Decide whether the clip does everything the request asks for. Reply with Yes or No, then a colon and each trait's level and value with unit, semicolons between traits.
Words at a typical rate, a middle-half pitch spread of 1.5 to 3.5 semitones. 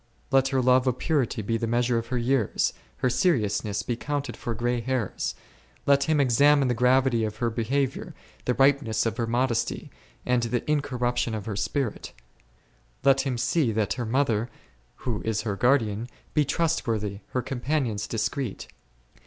Yes: average, 170 wpm; average, 3.0 semitones